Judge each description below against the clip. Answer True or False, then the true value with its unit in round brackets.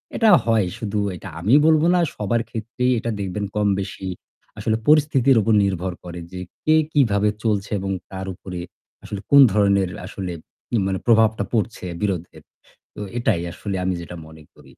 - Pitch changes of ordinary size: True (3.4 semitones)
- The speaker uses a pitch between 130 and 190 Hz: False (105 Hz)